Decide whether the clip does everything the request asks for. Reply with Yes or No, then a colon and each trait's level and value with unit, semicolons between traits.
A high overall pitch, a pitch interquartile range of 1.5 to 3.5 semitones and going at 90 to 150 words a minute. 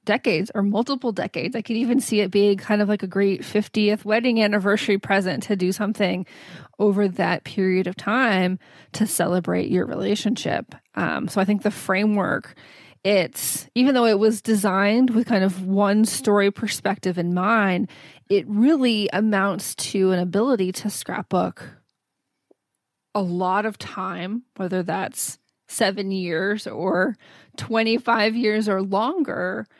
Yes: high, 205 Hz; narrow, 2.5 semitones; average, 145 wpm